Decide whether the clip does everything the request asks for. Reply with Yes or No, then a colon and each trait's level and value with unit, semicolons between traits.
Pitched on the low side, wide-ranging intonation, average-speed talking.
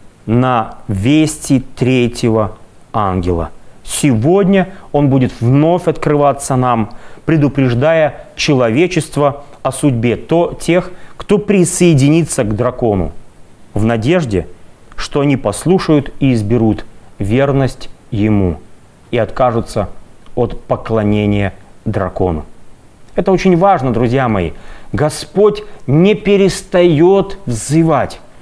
No: low, 130 Hz; wide, 6.4 semitones; slow, 90 wpm